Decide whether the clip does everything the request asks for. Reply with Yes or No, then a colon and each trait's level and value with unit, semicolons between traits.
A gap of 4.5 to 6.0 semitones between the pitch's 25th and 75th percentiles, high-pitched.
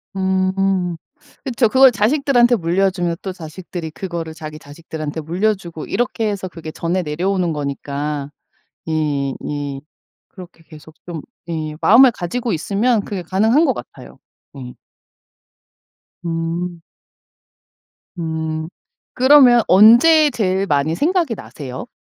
No: average, 5.3 semitones; medium, 175 Hz